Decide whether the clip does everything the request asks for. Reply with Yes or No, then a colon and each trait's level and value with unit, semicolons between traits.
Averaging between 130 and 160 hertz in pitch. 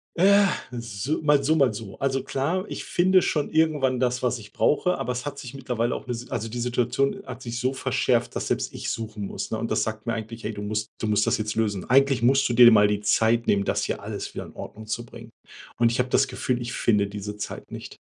No: low, 120 Hz